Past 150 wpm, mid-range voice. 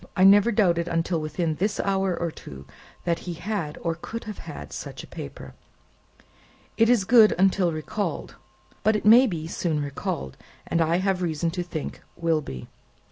Yes: average, 170 wpm; medium, 175 Hz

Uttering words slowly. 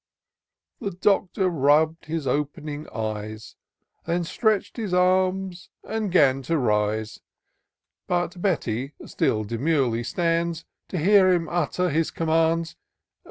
Yes: slow, 115 wpm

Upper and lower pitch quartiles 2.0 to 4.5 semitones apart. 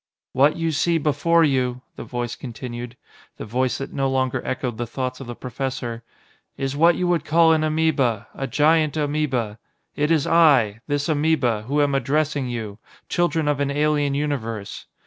Yes: average, 3.7 semitones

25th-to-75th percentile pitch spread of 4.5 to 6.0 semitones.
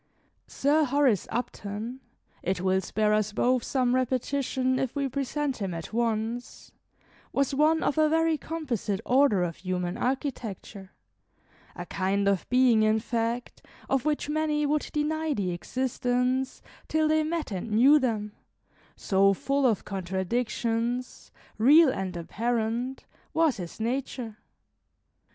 Yes: average, 5.0 semitones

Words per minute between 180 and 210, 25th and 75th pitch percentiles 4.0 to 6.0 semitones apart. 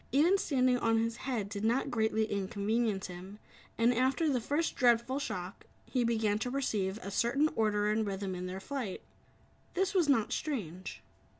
No: average, 170 wpm; average, 4.5 semitones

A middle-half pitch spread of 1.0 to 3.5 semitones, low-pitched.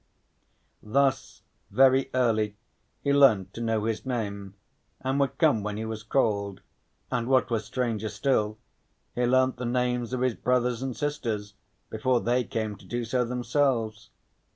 Yes: average, 3.0 semitones; low, 120 Hz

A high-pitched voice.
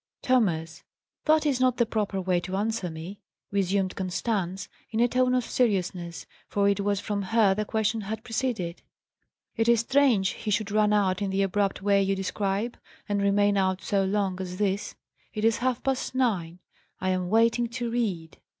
Yes: high, 205 Hz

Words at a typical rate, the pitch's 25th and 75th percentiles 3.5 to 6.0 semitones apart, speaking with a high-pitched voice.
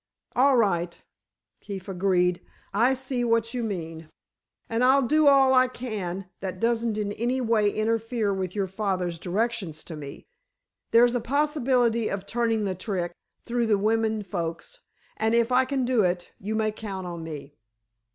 Yes: average, 160 wpm; average, 4.4 semitones; high, 220 Hz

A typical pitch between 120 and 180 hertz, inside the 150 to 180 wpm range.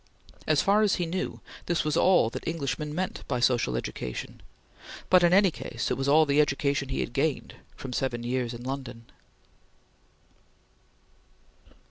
Yes: medium, 140 Hz; average, 155 wpm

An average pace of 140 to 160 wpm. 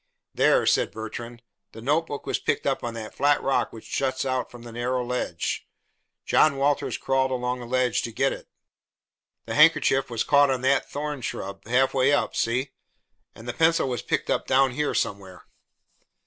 No: average, 175 wpm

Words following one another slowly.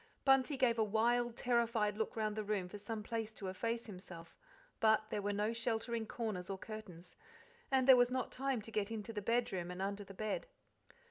No: average, 200 wpm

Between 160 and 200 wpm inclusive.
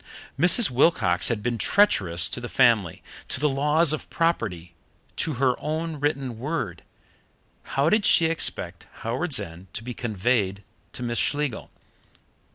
No: average, 145 wpm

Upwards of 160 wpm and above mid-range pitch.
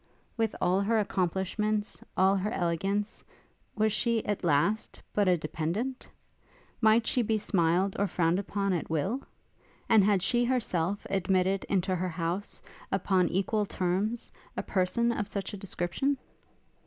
No: average, 140 wpm; high, 195 Hz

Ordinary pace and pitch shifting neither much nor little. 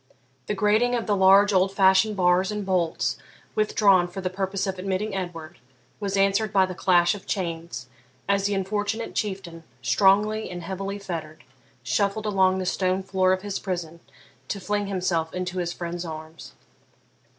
No: average, 160 wpm; narrow, 2.2 semitones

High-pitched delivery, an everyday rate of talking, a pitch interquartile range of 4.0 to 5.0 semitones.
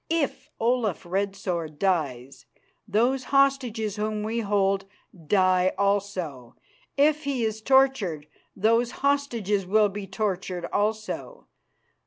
No: high, 210 Hz; slow, 110 wpm; average, 4.5 semitones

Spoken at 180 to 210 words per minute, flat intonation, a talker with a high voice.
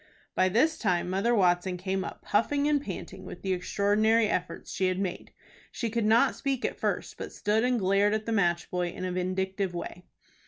No: average, 200 wpm; average, 3.5 semitones; high, 195 Hz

